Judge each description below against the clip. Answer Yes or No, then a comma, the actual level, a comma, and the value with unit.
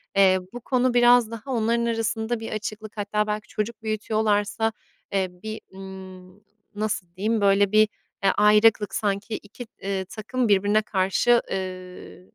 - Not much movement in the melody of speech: Yes, narrow, 2.2 semitones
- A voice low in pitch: No, high, 210 Hz